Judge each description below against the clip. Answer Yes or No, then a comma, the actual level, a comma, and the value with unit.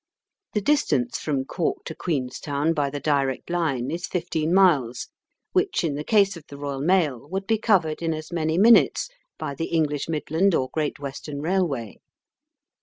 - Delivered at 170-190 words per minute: Yes, average, 175 wpm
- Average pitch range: Yes, average, 4.1 semitones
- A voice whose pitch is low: No, medium, 155 Hz